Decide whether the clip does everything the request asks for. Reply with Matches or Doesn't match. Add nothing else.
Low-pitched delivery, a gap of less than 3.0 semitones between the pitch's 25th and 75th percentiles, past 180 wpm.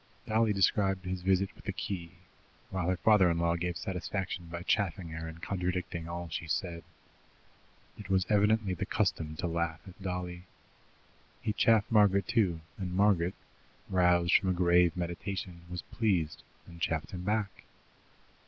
Doesn't match